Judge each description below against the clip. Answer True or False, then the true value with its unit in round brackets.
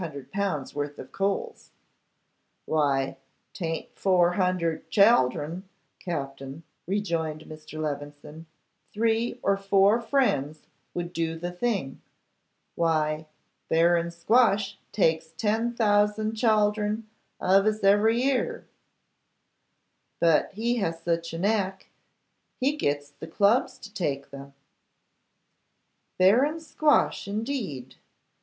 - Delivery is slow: True (100 wpm)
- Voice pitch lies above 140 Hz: True (185 Hz)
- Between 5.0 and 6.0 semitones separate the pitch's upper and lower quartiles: True (5.4 semitones)